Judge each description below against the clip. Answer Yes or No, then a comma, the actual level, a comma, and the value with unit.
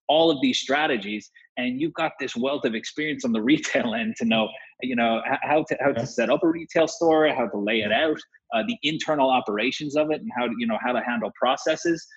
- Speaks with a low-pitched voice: No, medium, 155 Hz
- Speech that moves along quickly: Yes, fast, 235 wpm